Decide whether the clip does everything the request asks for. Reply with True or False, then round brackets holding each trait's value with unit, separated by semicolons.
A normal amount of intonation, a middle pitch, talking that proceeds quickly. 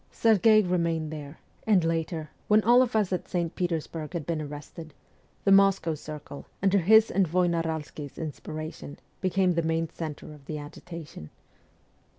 False (3.3 semitones; 165 Hz; 145 wpm)